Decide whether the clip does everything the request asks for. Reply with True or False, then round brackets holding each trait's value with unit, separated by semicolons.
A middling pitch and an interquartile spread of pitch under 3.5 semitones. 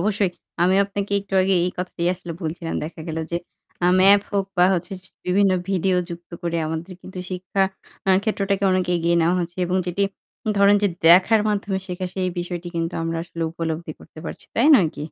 True (180 Hz; 2.5 semitones)